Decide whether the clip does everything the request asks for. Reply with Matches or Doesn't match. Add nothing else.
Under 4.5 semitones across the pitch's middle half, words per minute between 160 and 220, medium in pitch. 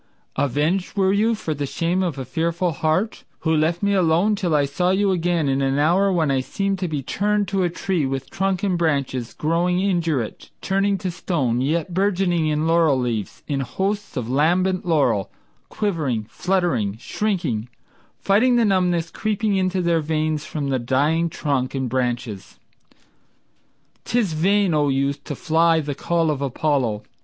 Doesn't match